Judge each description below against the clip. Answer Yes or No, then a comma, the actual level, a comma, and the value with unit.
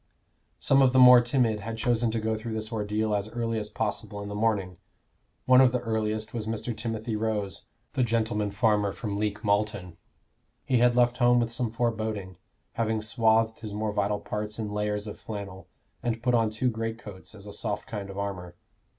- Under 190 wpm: No, average, 195 wpm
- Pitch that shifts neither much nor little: No, narrow, 1.9 semitones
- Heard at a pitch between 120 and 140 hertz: No, low, 110 Hz